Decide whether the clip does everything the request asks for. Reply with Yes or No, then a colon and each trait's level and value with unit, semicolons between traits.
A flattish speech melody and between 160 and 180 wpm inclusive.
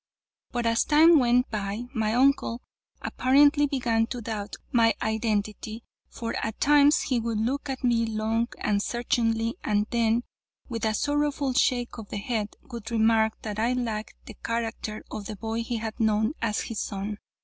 Yes: narrow, 2.1 semitones; average, 170 wpm